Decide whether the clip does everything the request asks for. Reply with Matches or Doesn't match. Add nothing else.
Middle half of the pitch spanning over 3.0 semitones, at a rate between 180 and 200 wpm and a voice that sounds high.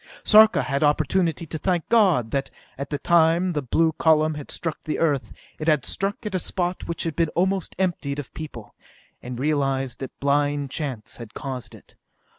Doesn't match